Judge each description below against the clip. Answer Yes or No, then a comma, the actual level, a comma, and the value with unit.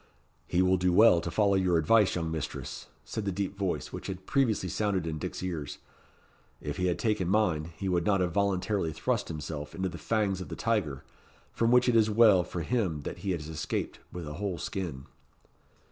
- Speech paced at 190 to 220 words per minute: Yes, fast, 205 wpm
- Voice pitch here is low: Yes, very low, 95 Hz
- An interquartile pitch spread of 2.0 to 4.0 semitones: Yes, average, 3.7 semitones